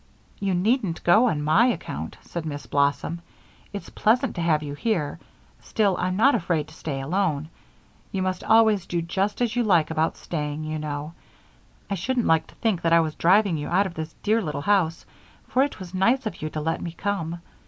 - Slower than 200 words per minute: No, fast, 205 wpm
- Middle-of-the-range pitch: Yes, medium, 175 Hz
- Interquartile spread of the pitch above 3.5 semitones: Yes, average, 4.9 semitones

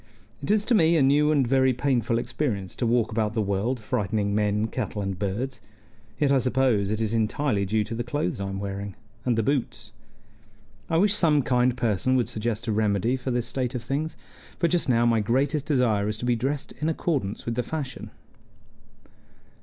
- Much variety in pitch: No, average, 4.2 semitones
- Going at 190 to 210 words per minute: Yes, average, 200 wpm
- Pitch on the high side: No, low, 120 Hz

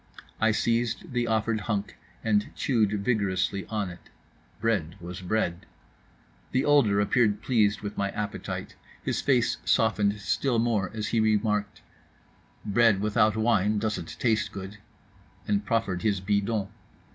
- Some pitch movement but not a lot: No, narrow, 2.2 semitones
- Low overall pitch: Yes, low, 105 Hz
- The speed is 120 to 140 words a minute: Yes, slow, 135 wpm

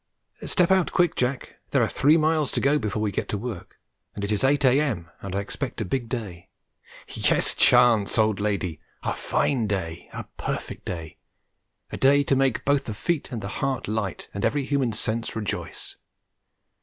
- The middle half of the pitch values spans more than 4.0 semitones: Yes, wide, 5.4 semitones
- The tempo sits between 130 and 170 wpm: No, average, 185 wpm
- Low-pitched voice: Yes, low, 115 Hz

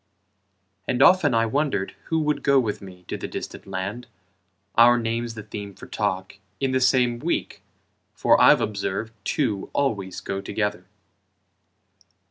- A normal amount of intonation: Yes, average, 4.5 semitones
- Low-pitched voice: Yes, low, 115 Hz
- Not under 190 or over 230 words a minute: No, average, 145 wpm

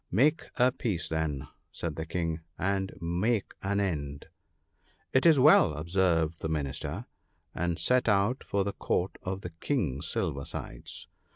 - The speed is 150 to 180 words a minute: Yes, average, 165 wpm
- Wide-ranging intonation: No, average, 4.2 semitones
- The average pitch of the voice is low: Yes, very low, 90 Hz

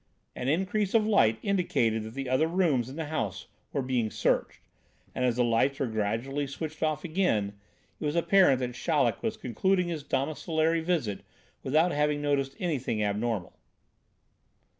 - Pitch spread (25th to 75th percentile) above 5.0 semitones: Yes, wide, 5.5 semitones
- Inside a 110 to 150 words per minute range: No, average, 160 wpm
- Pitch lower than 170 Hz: Yes, medium, 140 Hz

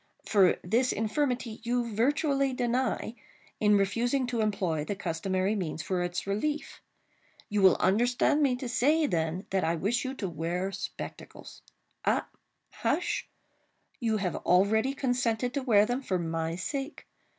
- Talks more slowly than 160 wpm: Yes, average, 140 wpm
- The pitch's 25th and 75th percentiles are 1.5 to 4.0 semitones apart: No, average, 5.2 semitones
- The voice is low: No, high, 220 Hz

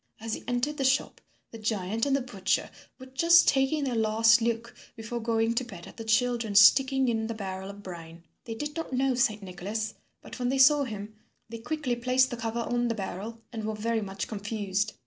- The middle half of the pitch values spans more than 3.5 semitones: No, average, 3.2 semitones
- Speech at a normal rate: No, fast, 210 wpm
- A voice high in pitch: Yes, high, 230 Hz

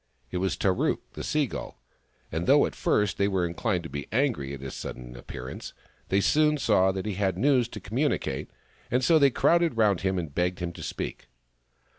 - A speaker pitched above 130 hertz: No, very low, 95 Hz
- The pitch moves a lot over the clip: Yes, wide, 6.0 semitones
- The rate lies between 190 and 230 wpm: Yes, average, 200 wpm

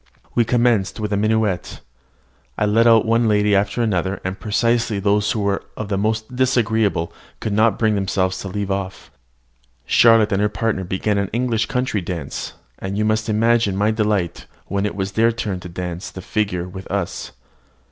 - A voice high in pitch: No, low, 105 Hz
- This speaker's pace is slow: No, average, 180 wpm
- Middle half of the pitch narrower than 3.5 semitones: Yes, narrow, 2.5 semitones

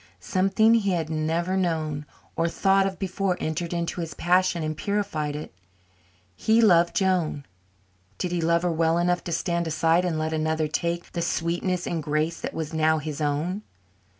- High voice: No, medium, 170 Hz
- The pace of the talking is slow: No, average, 175 wpm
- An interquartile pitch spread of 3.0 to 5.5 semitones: No, narrow, 2.5 semitones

